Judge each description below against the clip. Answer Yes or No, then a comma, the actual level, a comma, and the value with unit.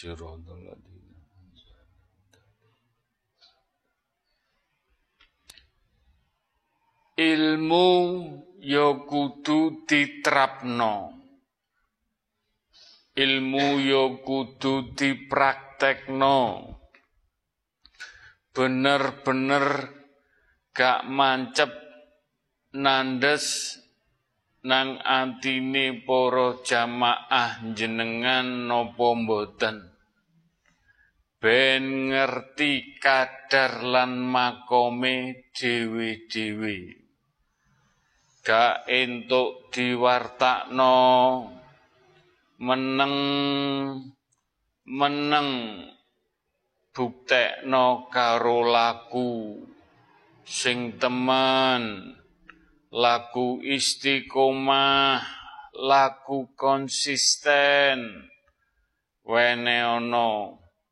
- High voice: No, low, 130 Hz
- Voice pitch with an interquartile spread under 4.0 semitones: Yes, narrow, 2.5 semitones